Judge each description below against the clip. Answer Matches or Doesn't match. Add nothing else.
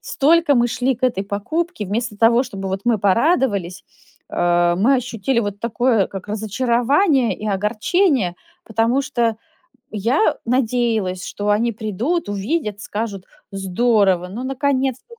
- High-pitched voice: Matches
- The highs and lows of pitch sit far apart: Doesn't match